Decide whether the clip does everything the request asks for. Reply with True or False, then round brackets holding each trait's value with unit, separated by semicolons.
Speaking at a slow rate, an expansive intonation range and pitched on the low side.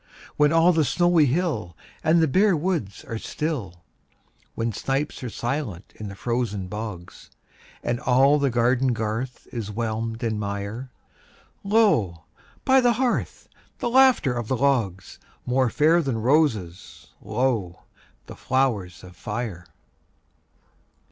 True (130 wpm; 6.1 semitones; 125 Hz)